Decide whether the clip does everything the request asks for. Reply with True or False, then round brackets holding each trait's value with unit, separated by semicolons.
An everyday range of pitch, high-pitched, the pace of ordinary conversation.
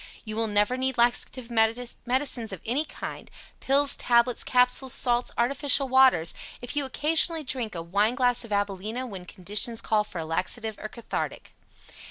True (3.4 semitones; 240 Hz; 160 wpm)